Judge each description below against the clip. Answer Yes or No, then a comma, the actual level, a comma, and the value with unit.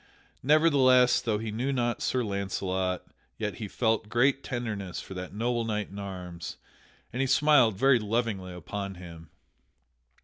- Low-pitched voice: Yes, low, 110 Hz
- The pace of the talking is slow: No, average, 145 wpm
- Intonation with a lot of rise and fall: No, average, 4.5 semitones